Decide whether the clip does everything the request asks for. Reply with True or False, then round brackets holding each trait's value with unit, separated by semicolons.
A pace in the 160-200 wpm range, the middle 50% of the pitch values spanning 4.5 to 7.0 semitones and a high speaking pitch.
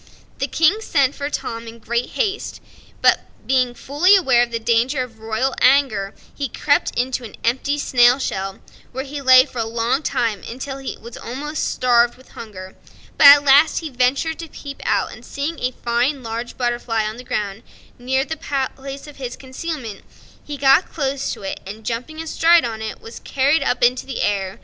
False (190 wpm; 3.3 semitones; 255 Hz)